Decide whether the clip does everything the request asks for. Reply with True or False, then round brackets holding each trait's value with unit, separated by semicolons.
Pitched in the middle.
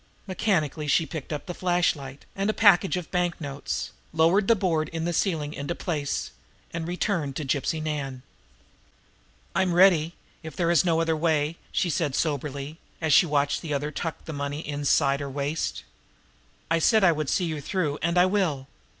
True (160 Hz)